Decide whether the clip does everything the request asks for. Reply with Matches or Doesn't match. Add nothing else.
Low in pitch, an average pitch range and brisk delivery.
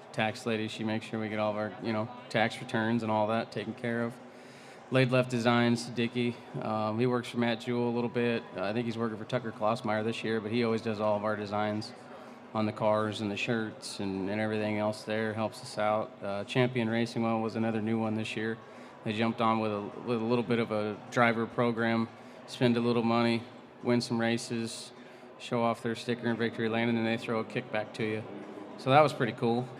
Doesn't match